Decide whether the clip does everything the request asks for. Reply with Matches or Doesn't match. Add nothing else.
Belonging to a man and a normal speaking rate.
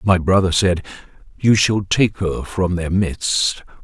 Matches